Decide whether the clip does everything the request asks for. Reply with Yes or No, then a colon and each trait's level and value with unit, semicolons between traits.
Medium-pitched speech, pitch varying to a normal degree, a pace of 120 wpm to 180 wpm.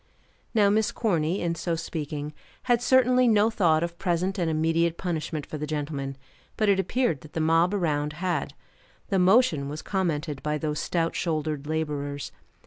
Yes: medium, 165 Hz; average, 4.1 semitones; average, 165 wpm